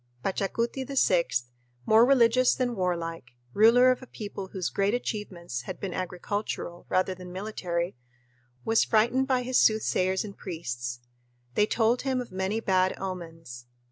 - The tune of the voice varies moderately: Yes, average, 4.6 semitones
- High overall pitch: Yes, high, 195 Hz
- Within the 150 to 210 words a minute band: No, average, 140 wpm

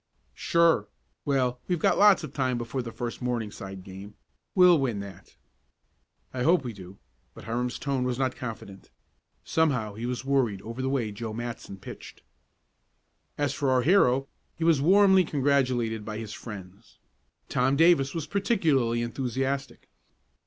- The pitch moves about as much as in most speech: Yes, average, 4.1 semitones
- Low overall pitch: Yes, low, 125 Hz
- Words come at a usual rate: Yes, average, 150 wpm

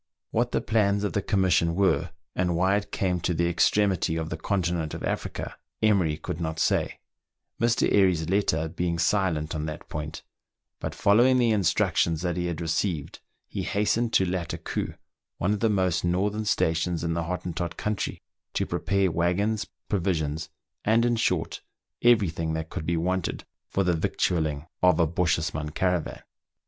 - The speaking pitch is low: Yes, very low, 90 Hz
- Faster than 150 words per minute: Yes, average, 165 wpm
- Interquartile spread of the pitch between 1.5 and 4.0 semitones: Yes, average, 3.7 semitones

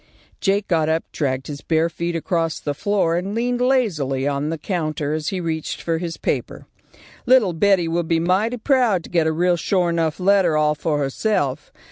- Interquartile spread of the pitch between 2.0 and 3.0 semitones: No, average, 4.0 semitones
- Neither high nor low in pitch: Yes, medium, 170 Hz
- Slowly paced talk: No, average, 190 wpm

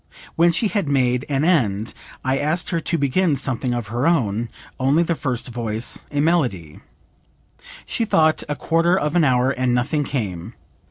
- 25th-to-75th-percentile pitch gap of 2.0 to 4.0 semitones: No, average, 5.2 semitones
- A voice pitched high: No, low, 135 Hz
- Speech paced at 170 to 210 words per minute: Yes, average, 175 wpm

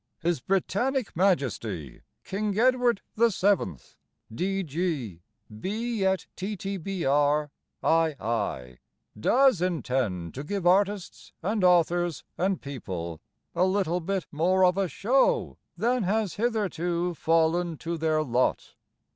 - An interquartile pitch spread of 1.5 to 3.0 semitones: No, average, 5.1 semitones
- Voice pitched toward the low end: No, medium, 175 Hz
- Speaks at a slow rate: Yes, slow, 105 wpm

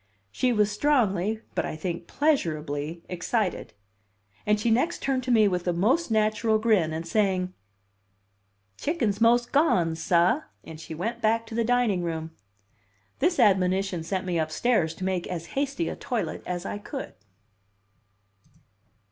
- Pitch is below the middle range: No, high, 205 Hz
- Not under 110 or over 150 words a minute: Yes, average, 145 wpm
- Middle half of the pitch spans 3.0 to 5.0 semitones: No, wide, 5.4 semitones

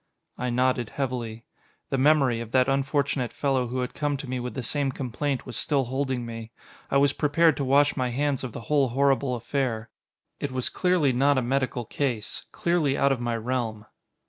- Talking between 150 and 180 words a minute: No, average, 195 wpm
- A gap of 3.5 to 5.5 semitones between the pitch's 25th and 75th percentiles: No, narrow, 2.6 semitones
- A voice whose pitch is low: Yes, low, 130 Hz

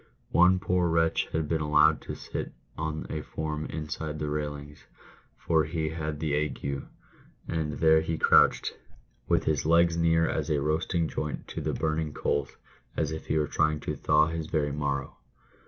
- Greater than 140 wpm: Yes, average, 170 wpm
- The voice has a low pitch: Yes, very low, 80 Hz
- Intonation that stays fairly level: Yes, narrow, 1.3 semitones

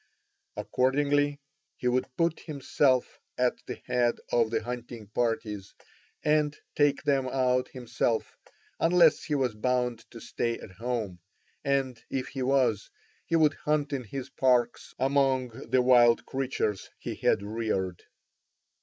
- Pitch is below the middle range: Yes, low, 125 Hz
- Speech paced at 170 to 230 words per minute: No, slow, 135 wpm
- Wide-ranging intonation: No, average, 2.9 semitones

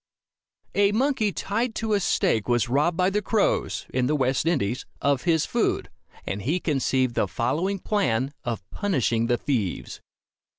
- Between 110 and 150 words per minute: No, average, 160 wpm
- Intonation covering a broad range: Yes, wide, 8.5 semitones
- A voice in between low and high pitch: Yes, medium, 145 Hz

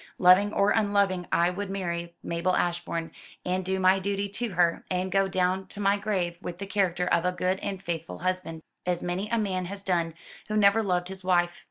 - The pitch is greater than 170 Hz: Yes, medium, 185 Hz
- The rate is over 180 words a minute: Yes, fast, 205 wpm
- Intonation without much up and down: Yes, narrow, 2.1 semitones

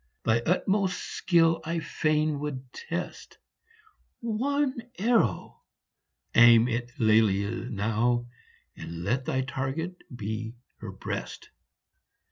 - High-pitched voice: No, low, 130 Hz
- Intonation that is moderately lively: No, wide, 6.8 semitones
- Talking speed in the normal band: No, slow, 95 wpm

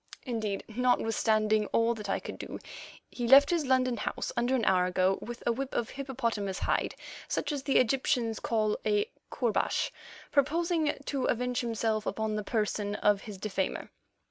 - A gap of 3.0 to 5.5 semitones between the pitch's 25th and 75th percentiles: Yes, average, 3.4 semitones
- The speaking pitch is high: Yes, high, 230 Hz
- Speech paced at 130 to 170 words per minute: Yes, average, 165 wpm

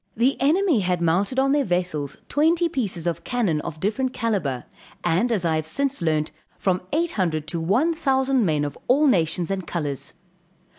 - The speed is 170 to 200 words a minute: Yes, average, 180 wpm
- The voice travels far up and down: Yes, wide, 8.5 semitones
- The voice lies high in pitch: Yes, high, 195 Hz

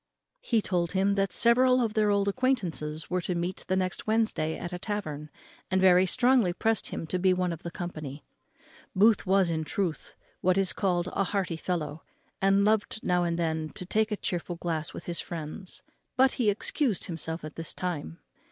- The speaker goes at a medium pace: Yes, average, 190 wpm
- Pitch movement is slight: No, average, 3.4 semitones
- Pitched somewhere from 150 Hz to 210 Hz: Yes, medium, 185 Hz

